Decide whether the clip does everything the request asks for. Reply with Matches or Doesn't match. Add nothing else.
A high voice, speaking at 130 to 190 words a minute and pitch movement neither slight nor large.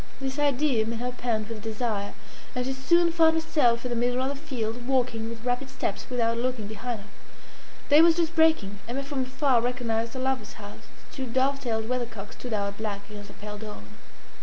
Doesn't match